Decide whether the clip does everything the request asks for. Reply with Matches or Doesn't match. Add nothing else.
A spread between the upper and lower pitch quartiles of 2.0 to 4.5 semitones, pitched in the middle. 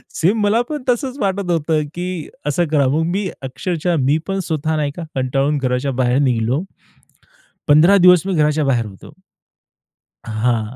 Doesn't match